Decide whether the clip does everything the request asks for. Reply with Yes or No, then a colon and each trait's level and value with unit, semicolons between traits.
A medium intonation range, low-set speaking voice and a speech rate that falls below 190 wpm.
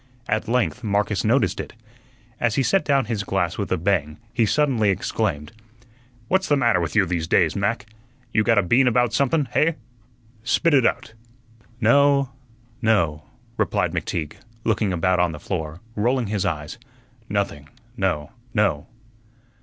No: wide, 5.8 semitones; low, 105 Hz; average, 155 wpm